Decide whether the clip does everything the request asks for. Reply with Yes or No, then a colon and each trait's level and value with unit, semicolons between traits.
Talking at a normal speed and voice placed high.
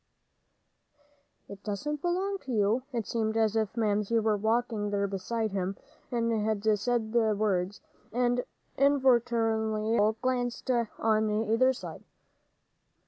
No: slow, 125 wpm; high, 220 Hz